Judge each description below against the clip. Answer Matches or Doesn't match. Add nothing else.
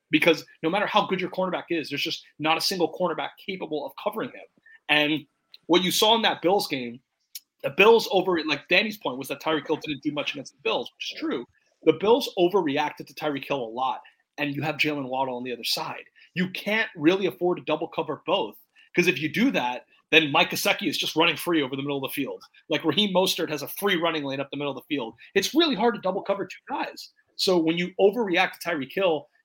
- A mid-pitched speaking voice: Matches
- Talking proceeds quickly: Matches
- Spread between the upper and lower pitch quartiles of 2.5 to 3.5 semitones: Doesn't match